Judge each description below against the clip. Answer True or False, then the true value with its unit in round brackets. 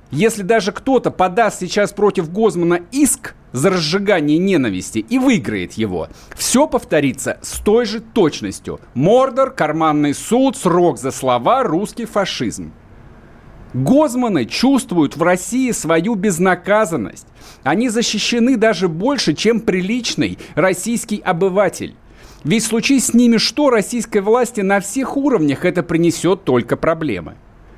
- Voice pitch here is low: False (205 Hz)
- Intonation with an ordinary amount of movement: False (5.8 semitones)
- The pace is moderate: True (120 wpm)